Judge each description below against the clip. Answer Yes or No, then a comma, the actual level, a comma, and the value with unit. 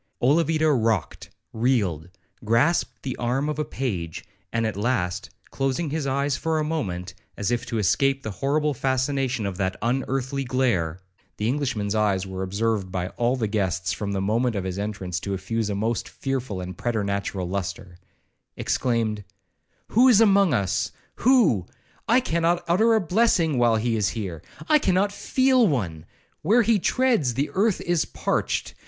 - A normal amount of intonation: No, wide, 7.2 semitones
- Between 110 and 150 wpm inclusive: No, average, 160 wpm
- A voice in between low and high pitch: No, low, 120 Hz